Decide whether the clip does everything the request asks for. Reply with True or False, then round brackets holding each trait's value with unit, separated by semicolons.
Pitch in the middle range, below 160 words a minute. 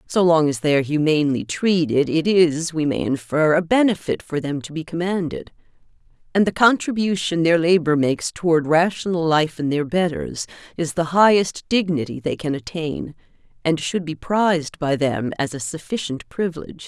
False (160 Hz; 170 wpm)